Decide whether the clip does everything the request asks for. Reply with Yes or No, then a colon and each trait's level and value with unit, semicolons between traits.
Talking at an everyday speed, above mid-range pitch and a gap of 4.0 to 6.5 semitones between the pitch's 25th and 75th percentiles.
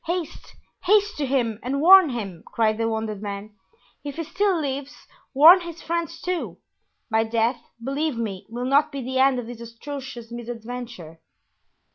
Yes: average, 160 wpm; very high, 255 Hz; average, 5.2 semitones